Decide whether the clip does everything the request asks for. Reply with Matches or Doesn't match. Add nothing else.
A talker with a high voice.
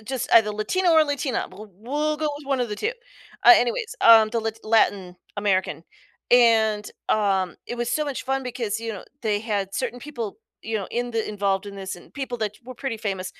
Matches